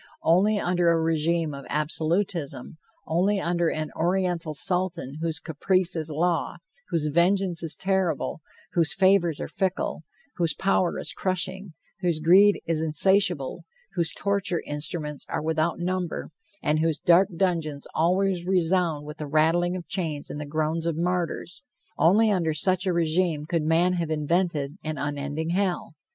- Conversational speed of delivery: Yes, average, 150 wpm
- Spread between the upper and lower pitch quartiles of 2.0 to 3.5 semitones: Yes, average, 2.8 semitones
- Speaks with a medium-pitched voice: Yes, medium, 170 Hz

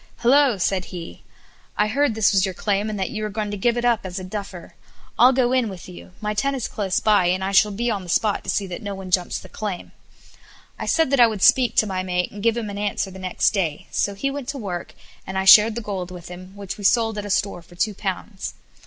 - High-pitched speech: Yes, high, 205 Hz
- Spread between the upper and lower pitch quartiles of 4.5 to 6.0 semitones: No, average, 3.0 semitones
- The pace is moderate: No, fast, 265 wpm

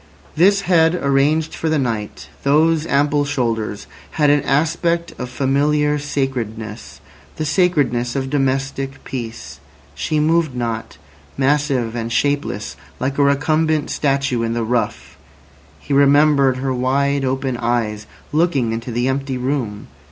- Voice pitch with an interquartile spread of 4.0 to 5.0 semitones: No, average, 3.4 semitones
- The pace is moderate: No, slow, 130 wpm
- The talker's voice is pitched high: No, low, 135 Hz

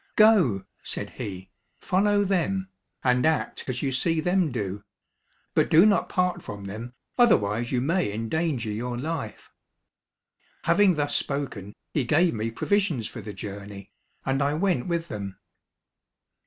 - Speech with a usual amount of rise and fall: No, wide, 8.2 semitones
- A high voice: No, low, 135 Hz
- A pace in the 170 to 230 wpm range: No, average, 140 wpm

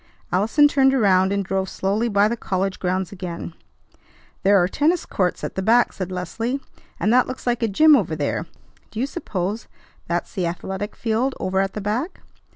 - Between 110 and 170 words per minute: No, average, 185 wpm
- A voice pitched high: Yes, high, 200 Hz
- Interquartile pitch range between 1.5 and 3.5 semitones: No, average, 4.3 semitones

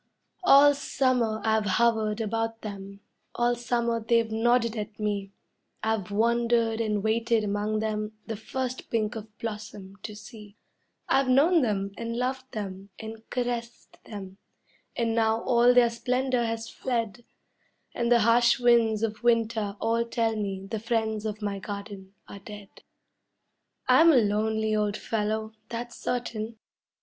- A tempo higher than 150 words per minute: No, average, 140 wpm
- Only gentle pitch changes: Yes, narrow, 2.1 semitones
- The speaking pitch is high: Yes, high, 225 Hz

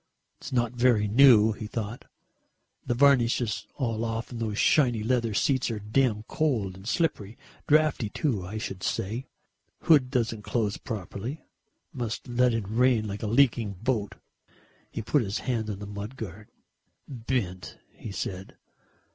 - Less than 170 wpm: Yes, average, 155 wpm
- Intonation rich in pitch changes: No, average, 3.3 semitones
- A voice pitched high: No, low, 115 Hz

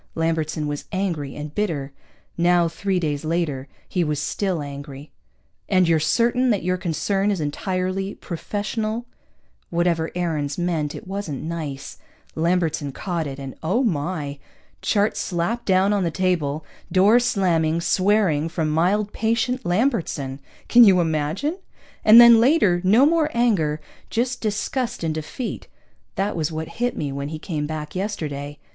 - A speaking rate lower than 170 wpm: Yes, average, 145 wpm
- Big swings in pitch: No, average, 5.0 semitones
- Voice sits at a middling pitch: Yes, medium, 175 Hz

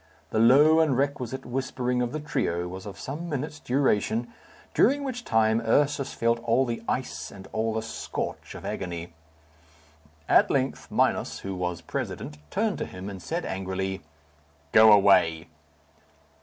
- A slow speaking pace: No, average, 150 wpm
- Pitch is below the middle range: Yes, low, 115 Hz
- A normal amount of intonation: No, wide, 6.2 semitones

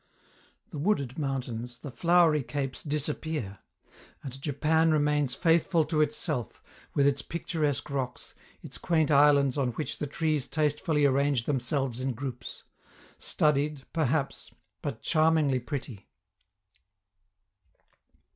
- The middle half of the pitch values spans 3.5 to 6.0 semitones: No, average, 2.7 semitones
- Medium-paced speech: No, slow, 110 wpm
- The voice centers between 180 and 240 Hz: No, medium, 145 Hz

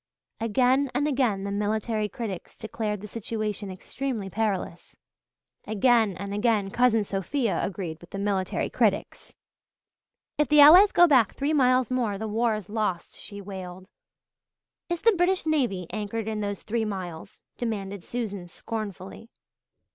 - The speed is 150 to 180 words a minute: No, average, 140 wpm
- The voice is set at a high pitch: Yes, high, 215 Hz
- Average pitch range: Yes, average, 3.8 semitones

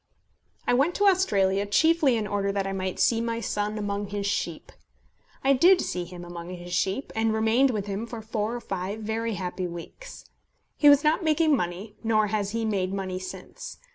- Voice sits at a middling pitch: No, high, 210 Hz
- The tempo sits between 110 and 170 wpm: No, average, 195 wpm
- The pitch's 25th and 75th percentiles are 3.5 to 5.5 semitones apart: Yes, average, 3.8 semitones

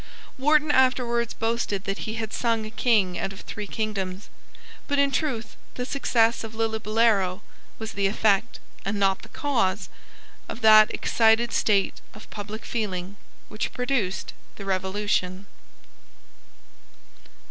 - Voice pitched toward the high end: Yes, high, 220 Hz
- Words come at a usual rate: No, slow, 130 wpm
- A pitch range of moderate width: Yes, average, 3.0 semitones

